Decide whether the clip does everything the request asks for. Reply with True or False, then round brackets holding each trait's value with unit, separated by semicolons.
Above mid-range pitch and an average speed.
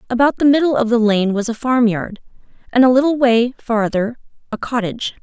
True (235 Hz; 185 wpm)